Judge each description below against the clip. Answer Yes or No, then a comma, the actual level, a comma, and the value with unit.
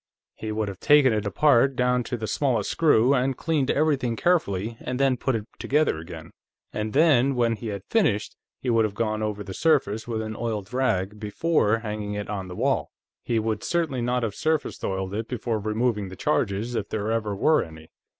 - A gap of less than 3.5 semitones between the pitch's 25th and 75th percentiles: No, average, 4.1 semitones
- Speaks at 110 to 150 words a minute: No, average, 200 wpm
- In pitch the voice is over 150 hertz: No, low, 115 Hz